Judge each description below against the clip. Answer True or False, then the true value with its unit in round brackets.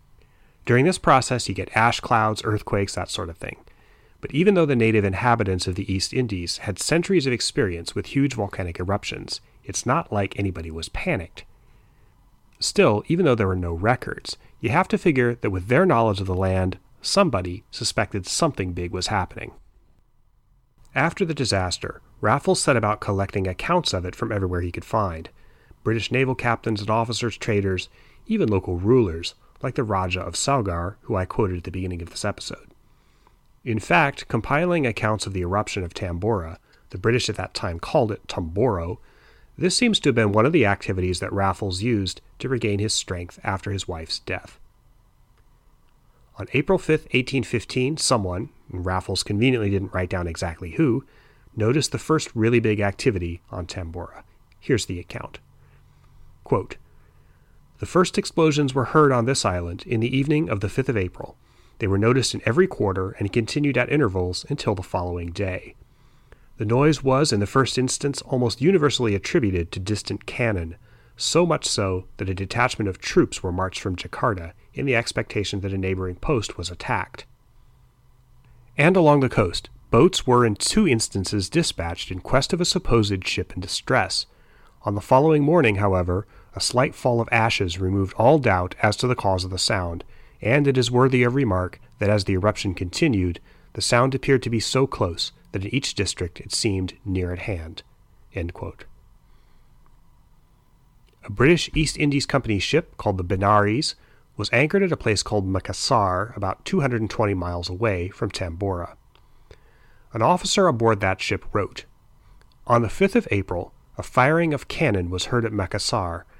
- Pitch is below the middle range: True (110 Hz)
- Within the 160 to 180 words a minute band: True (175 wpm)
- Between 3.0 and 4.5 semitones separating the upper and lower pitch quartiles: False (5.3 semitones)